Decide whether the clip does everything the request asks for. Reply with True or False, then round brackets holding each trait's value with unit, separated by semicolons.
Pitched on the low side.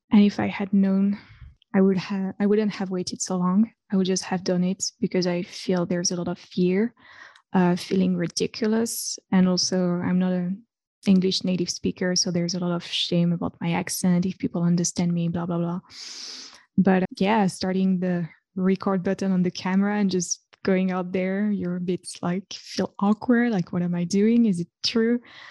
False (185 Hz)